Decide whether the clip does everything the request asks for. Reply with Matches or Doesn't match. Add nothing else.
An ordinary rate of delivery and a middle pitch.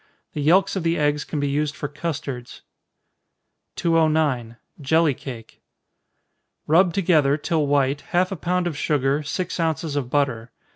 Matches